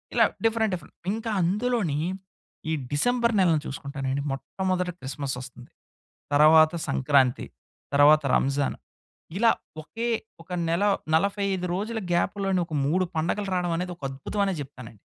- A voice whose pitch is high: No, medium, 170 Hz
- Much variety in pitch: Yes, wide, 5.9 semitones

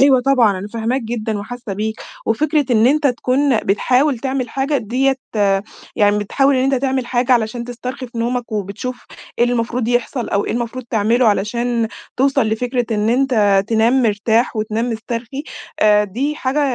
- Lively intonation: No, average, 3.0 semitones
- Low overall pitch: No, high, 240 Hz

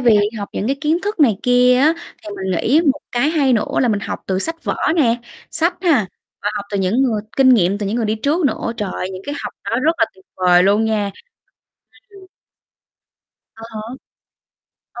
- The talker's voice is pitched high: Yes, high, 230 Hz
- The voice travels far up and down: Yes, wide, 6.0 semitones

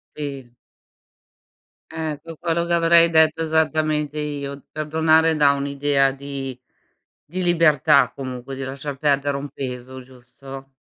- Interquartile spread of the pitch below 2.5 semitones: No, average, 2.8 semitones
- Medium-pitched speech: Yes, medium, 145 Hz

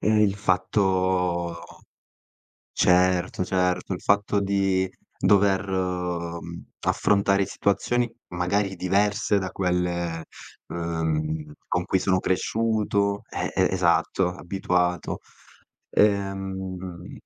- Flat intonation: Yes, narrow, 2.0 semitones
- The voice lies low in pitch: Yes, very low, 95 Hz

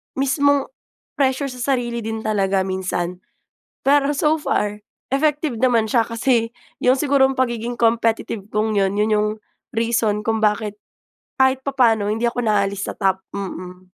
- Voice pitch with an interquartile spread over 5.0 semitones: No, average, 4.1 semitones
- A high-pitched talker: Yes, high, 230 Hz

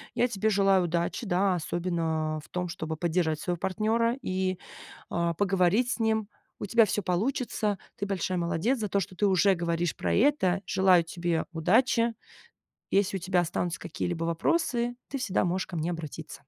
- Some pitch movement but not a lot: Yes, average, 3.8 semitones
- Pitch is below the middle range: No, medium, 185 Hz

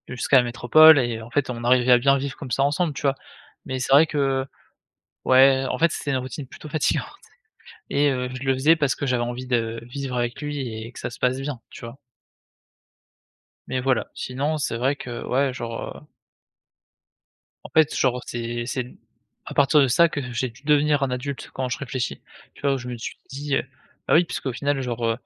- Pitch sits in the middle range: No, low, 130 Hz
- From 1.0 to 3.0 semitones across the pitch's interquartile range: Yes, narrow, 2.5 semitones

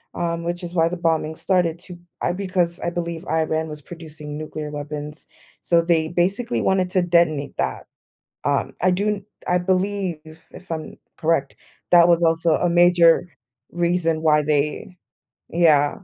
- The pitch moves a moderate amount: No, narrow, 2.1 semitones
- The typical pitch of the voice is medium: Yes, medium, 170 Hz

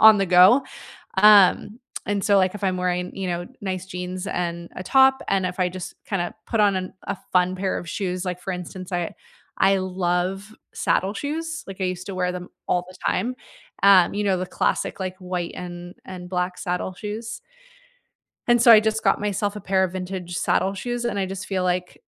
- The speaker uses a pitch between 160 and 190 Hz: Yes, medium, 185 Hz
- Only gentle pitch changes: Yes, narrow, 2.1 semitones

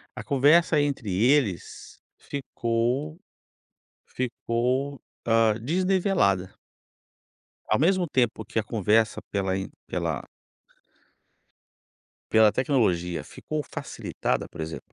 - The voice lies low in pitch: Yes, low, 120 Hz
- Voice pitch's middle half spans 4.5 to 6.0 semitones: Yes, wide, 5.5 semitones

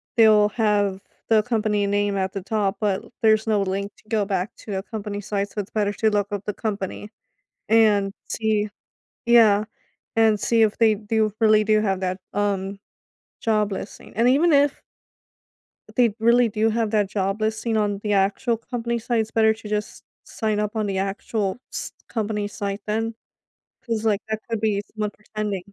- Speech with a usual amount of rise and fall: No, narrow, 1.6 semitones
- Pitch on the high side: Yes, high, 210 Hz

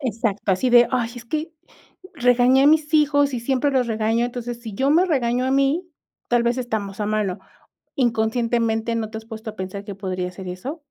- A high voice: Yes, high, 235 Hz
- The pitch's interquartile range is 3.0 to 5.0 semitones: Yes, average, 3.4 semitones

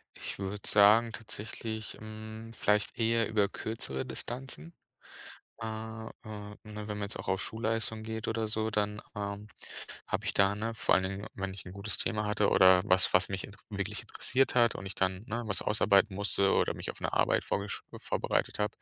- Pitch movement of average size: No, narrow, 1.9 semitones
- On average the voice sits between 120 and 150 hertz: No, low, 105 Hz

